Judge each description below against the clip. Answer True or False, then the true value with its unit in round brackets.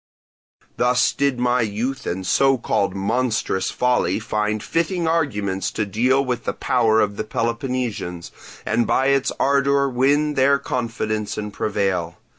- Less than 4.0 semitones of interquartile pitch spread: False (4.4 semitones)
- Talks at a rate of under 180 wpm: True (140 wpm)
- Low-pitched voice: True (120 Hz)